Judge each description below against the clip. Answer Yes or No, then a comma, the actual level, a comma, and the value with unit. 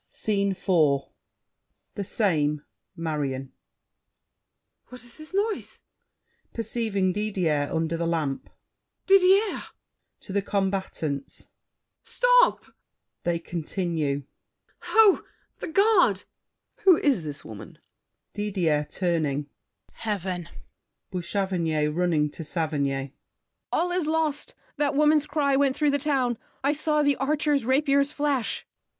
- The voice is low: No, high, 200 Hz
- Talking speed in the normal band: No, slow, 110 wpm